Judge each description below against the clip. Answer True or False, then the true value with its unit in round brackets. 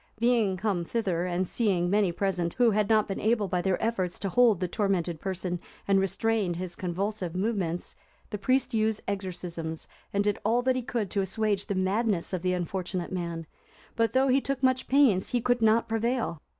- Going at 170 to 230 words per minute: True (190 wpm)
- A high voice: True (200 Hz)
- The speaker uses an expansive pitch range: False (3.8 semitones)